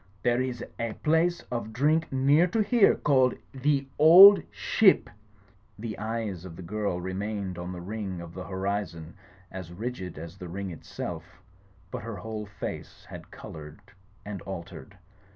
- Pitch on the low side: Yes, low, 105 Hz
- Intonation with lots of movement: Yes, wide, 6.1 semitones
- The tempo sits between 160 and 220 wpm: No, average, 150 wpm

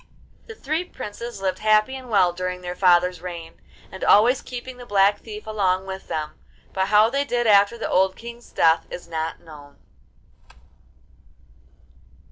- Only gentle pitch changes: No, average, 4.5 semitones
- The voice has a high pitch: Yes, high, 200 Hz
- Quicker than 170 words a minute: No, average, 155 wpm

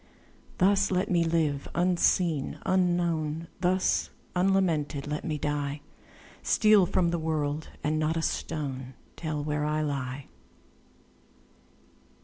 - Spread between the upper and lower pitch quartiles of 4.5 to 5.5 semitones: No, average, 3.2 semitones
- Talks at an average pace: No, slow, 115 wpm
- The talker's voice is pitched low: No, medium, 160 Hz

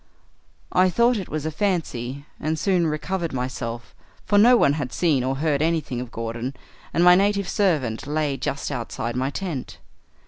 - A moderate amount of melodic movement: No, wide, 5.8 semitones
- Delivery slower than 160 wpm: No, average, 170 wpm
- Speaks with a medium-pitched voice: Yes, medium, 150 Hz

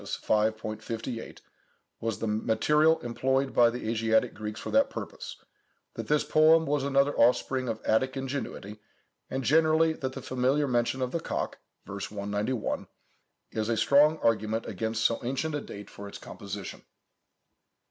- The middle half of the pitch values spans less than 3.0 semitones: No, average, 4.2 semitones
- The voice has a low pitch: Yes, low, 125 Hz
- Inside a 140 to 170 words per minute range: Yes, average, 150 wpm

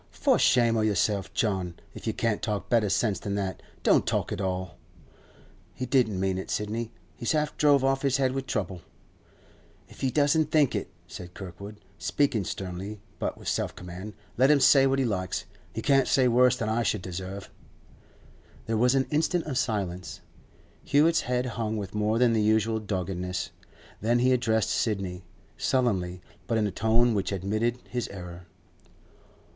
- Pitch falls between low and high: No, low, 110 Hz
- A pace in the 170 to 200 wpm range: Yes, average, 175 wpm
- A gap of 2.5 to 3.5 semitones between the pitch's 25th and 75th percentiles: No, average, 4.8 semitones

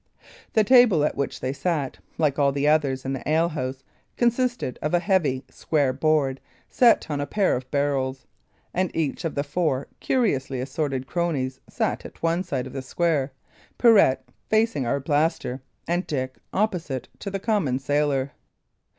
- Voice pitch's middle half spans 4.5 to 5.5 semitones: Yes, average, 4.8 semitones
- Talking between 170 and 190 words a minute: No, average, 160 wpm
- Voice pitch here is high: No, medium, 145 Hz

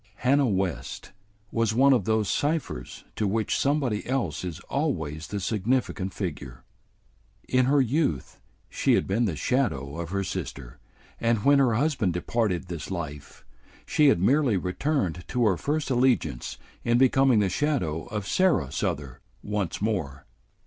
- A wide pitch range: Yes, wide, 7.3 semitones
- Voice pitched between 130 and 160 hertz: No, low, 105 Hz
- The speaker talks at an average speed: Yes, average, 150 wpm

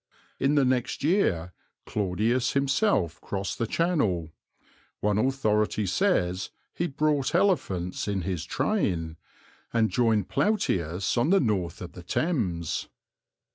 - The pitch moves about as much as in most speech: No, wide, 7.9 semitones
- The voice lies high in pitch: No, low, 110 Hz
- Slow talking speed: Yes, slow, 120 wpm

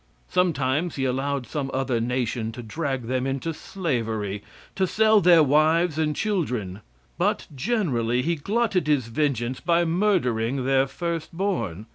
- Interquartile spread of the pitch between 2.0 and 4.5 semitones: No, wide, 5.6 semitones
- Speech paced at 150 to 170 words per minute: No, average, 140 wpm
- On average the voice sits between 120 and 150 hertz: Yes, medium, 140 Hz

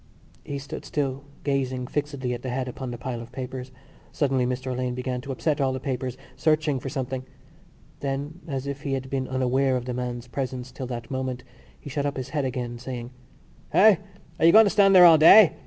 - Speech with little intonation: Yes, narrow, 2.0 semitones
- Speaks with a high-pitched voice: No, low, 130 Hz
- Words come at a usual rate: No, fast, 210 wpm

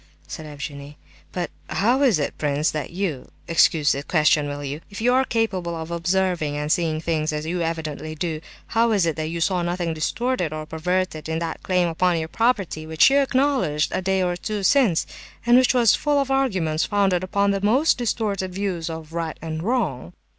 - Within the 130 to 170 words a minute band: No, average, 190 wpm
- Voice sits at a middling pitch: Yes, medium, 170 Hz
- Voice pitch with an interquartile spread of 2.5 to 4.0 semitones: No, average, 4.5 semitones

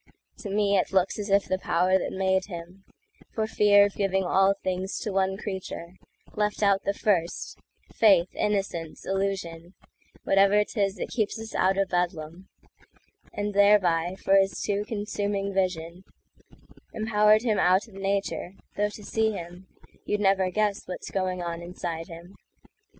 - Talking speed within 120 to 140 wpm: Yes, slow, 135 wpm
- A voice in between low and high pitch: No, high, 195 Hz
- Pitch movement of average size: No, narrow, 2.0 semitones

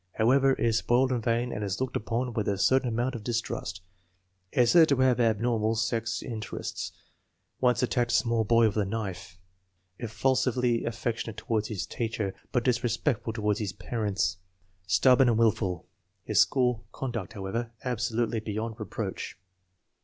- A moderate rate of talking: Yes, average, 160 wpm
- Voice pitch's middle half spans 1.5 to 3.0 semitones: Yes, narrow, 2.4 semitones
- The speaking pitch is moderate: No, low, 115 Hz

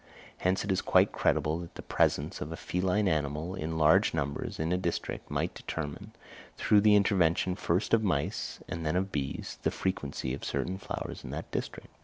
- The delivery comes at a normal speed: Yes, average, 190 wpm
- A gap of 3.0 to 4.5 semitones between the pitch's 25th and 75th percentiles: Yes, average, 3.6 semitones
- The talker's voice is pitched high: No, very low, 85 Hz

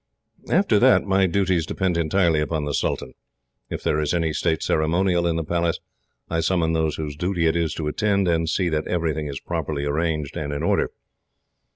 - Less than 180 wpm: No, average, 190 wpm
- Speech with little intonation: Yes, narrow, 2.2 semitones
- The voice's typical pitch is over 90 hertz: No, very low, 80 Hz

